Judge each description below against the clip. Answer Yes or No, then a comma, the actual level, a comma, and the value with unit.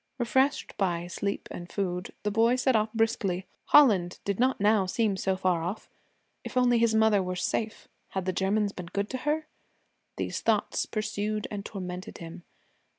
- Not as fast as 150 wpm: No, average, 170 wpm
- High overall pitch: Yes, high, 205 Hz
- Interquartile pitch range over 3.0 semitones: Yes, average, 3.5 semitones